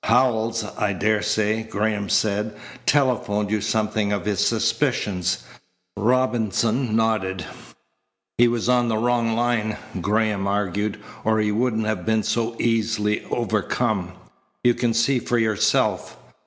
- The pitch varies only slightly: Yes, narrow, 1.9 semitones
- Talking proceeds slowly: Yes, slow, 125 wpm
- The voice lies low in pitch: Yes, low, 110 Hz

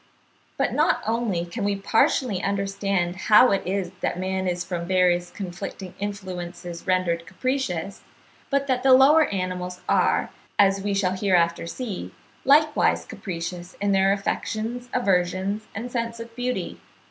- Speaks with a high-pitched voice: Yes, high, 195 Hz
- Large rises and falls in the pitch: No, average, 4.0 semitones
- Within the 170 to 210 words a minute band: No, average, 140 wpm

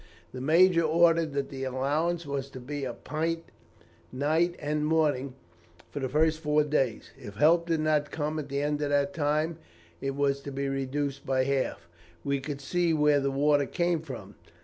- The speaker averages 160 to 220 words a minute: Yes, average, 185 wpm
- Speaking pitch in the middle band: Yes, medium, 145 Hz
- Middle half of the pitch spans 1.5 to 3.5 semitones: Yes, narrow, 2.5 semitones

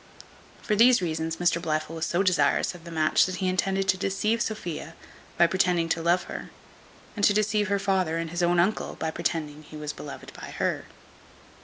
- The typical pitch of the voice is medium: Yes, medium, 175 Hz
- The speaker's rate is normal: Yes, average, 195 wpm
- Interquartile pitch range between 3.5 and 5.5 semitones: No, average, 3.0 semitones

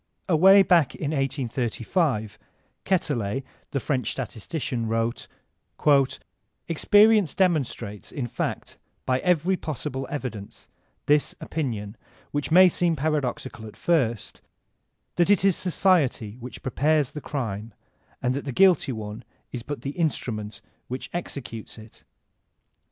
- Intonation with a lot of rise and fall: Yes, wide, 6.0 semitones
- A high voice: No, low, 135 Hz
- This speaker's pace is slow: Yes, slow, 120 wpm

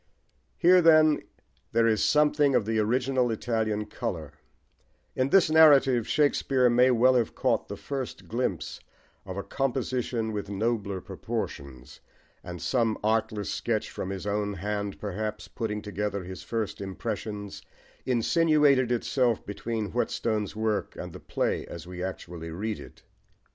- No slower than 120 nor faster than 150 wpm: Yes, average, 140 wpm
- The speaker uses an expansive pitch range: No, average, 3.9 semitones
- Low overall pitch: Yes, low, 110 Hz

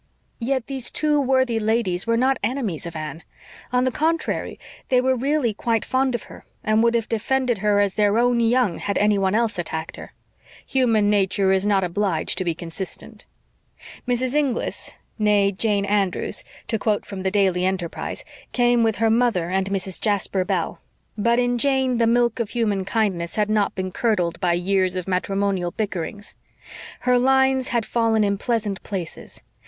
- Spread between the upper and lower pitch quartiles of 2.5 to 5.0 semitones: Yes, average, 4.1 semitones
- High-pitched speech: Yes, high, 210 Hz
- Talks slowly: No, average, 170 wpm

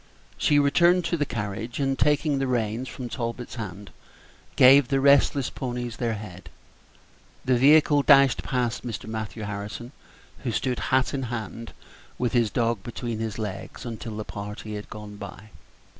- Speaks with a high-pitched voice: No, low, 120 Hz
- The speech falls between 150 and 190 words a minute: Yes, average, 160 wpm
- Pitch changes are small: No, average, 3.9 semitones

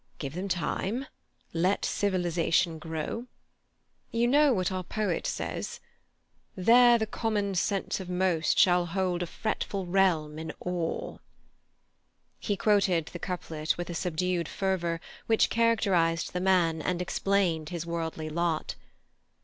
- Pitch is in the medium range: Yes, medium, 180 Hz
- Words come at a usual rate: No, slow, 130 wpm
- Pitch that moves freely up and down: No, average, 3.1 semitones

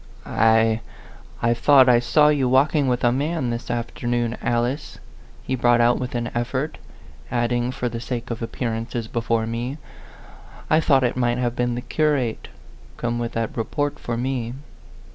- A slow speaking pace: No, average, 165 wpm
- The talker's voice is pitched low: Yes, low, 120 Hz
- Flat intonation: Yes, narrow, 1.8 semitones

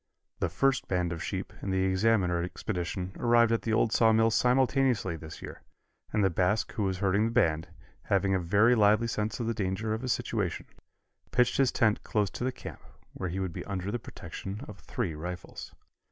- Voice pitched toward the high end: No, low, 105 Hz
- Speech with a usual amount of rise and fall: Yes, average, 3.8 semitones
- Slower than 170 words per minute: No, average, 195 wpm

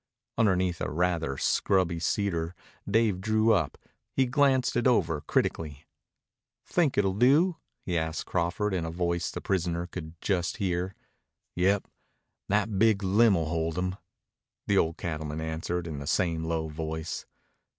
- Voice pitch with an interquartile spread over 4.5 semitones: No, average, 3.9 semitones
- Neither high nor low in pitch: No, very low, 90 Hz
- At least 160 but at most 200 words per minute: No, average, 140 wpm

